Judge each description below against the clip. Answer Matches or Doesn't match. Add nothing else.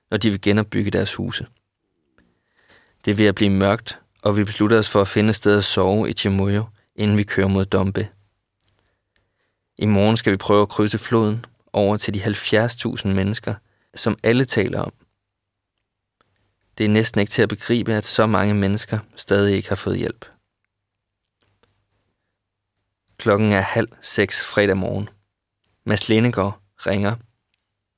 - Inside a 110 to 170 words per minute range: Matches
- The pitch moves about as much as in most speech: Doesn't match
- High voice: Doesn't match